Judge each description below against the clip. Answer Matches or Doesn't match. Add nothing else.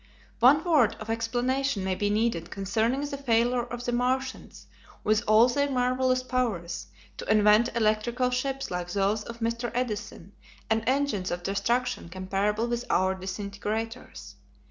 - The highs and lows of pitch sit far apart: Doesn't match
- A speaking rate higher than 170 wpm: Doesn't match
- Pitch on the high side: Matches